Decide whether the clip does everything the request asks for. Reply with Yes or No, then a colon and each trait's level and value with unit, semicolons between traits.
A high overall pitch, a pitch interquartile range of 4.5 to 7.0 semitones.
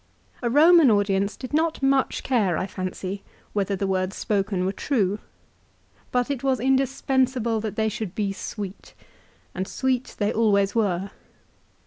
Yes: high, 215 Hz; average, 4.9 semitones